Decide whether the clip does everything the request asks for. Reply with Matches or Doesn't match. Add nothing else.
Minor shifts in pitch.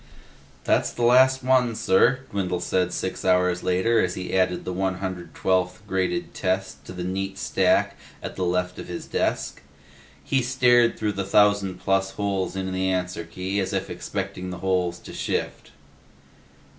Matches